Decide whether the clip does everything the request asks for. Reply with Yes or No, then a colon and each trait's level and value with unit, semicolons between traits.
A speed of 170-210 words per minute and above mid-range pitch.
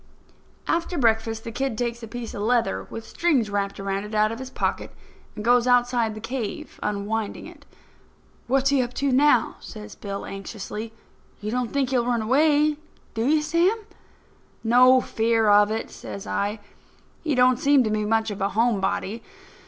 Yes: average, 175 wpm; high, 230 Hz